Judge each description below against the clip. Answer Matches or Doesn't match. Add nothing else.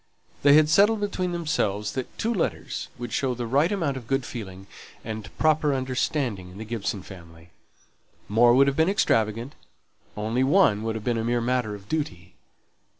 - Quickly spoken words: Doesn't match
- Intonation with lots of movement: Matches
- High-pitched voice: Doesn't match